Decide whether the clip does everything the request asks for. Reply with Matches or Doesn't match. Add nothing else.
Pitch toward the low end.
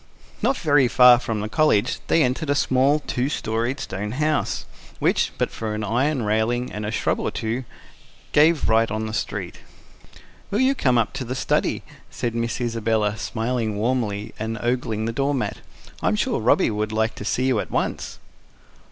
Matches